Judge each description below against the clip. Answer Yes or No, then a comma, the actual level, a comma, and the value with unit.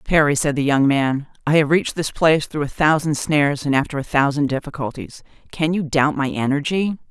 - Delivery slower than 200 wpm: No, fast, 205 wpm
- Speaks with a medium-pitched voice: Yes, medium, 145 Hz